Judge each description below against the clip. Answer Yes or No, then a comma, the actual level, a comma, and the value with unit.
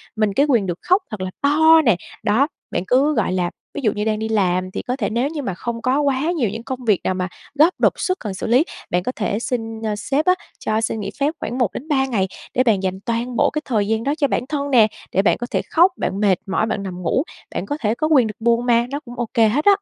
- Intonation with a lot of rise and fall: No, average, 5.0 semitones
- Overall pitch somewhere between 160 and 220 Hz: No, high, 235 Hz